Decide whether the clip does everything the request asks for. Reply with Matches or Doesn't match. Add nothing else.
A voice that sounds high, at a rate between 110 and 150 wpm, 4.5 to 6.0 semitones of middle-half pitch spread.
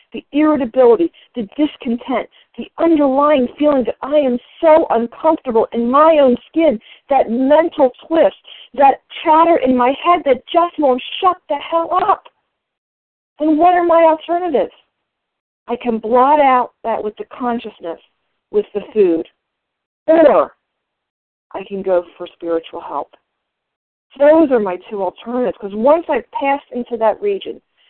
Matches